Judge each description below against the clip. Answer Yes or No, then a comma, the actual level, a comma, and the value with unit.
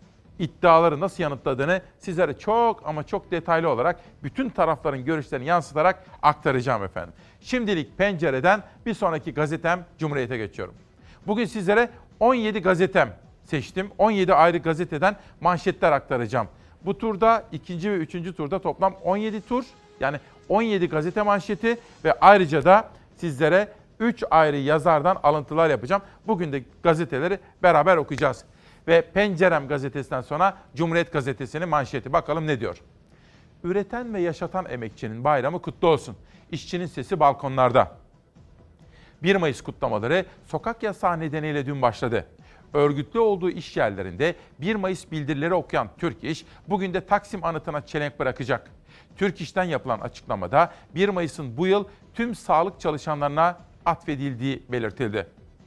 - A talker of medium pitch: Yes, medium, 170 Hz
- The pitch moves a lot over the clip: No, average, 4.5 semitones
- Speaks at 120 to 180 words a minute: Yes, average, 125 wpm